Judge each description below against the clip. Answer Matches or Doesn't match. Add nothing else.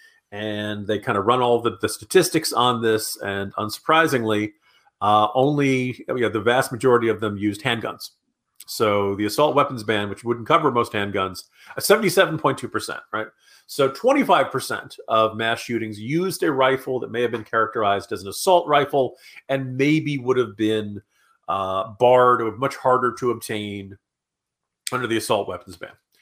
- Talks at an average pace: Matches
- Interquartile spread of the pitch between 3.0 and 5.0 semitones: Matches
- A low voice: Matches